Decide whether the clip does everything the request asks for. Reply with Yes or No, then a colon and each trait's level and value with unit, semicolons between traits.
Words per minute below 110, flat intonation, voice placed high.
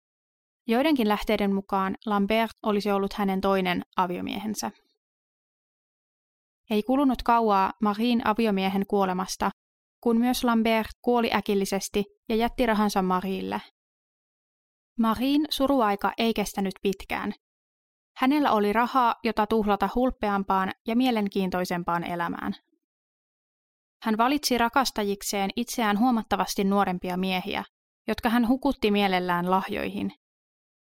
No: slow, 95 wpm; average, 3.3 semitones; high, 215 Hz